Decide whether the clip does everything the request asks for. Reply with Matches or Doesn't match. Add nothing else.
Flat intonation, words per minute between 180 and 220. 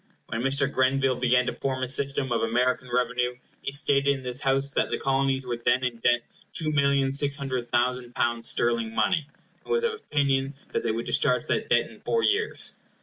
Matches